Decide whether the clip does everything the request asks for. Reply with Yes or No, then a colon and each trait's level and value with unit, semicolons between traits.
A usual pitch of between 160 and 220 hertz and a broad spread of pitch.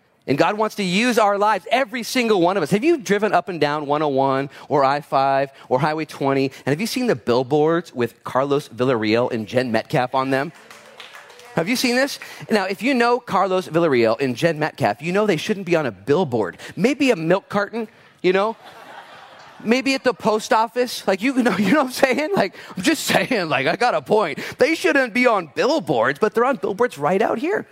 Yes: medium, 185 Hz; wide, 8.9 semitones